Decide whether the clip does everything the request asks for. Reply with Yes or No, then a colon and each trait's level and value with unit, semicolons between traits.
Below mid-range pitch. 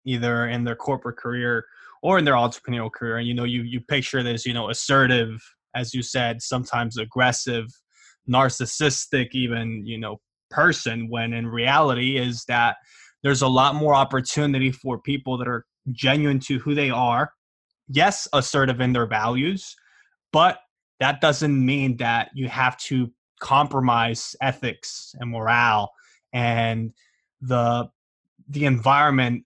Yes: low, 125 Hz